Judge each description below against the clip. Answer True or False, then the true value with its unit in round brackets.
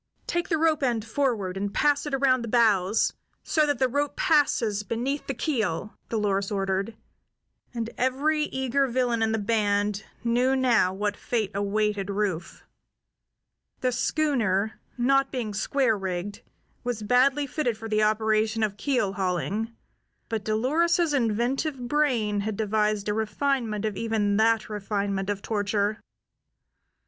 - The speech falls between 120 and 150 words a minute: True (140 wpm)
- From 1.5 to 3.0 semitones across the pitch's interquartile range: False (4.2 semitones)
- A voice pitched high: True (220 Hz)